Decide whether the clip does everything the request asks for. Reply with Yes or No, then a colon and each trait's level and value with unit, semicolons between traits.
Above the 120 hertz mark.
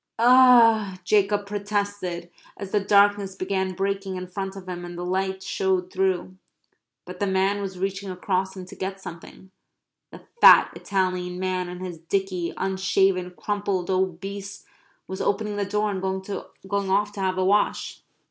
Yes: high, 190 Hz